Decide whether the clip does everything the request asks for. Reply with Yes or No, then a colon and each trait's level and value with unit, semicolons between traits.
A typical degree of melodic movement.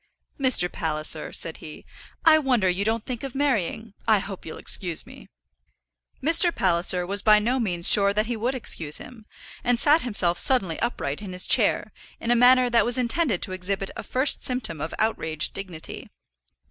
No: wide, 5.8 semitones